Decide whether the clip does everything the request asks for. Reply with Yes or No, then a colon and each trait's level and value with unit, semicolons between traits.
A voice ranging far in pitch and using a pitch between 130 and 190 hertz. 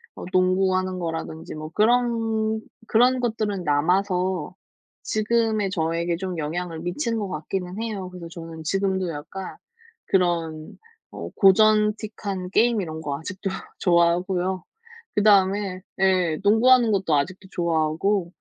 No: average, 3.6 semitones; medium, 185 Hz